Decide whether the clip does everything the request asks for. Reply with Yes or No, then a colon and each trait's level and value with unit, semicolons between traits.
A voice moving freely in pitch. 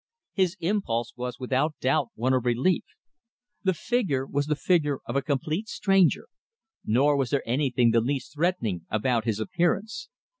Yes: wide, 5.8 semitones